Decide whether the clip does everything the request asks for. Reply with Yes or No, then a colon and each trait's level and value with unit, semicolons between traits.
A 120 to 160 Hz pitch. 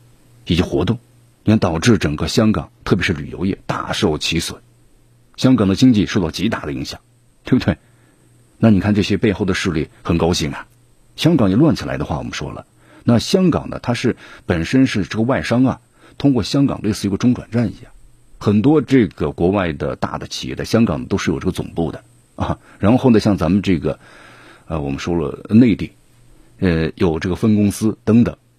No: low, 105 Hz